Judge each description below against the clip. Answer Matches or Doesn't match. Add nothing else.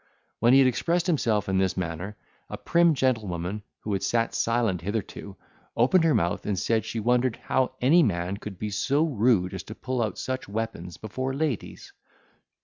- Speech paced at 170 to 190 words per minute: Matches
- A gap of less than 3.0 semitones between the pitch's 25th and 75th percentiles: Doesn't match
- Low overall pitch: Matches